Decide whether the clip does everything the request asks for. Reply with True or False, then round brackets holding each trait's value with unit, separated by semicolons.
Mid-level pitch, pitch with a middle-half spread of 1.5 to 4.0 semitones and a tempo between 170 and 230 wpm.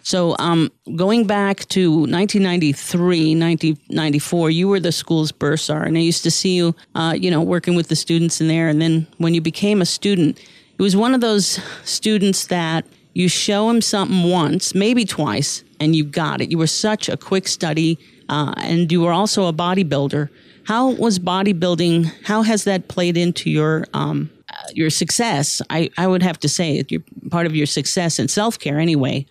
True (170 Hz; 3.3 semitones; 185 wpm)